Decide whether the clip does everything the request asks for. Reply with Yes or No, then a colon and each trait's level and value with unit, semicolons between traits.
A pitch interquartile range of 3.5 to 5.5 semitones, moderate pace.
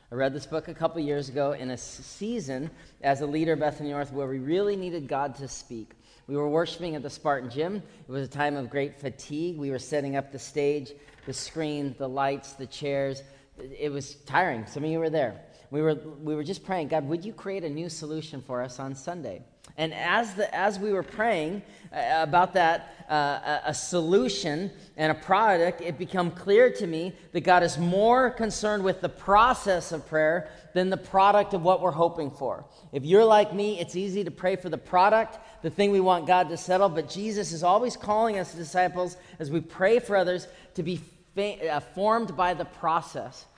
No: average, 4.5 semitones; fast, 210 wpm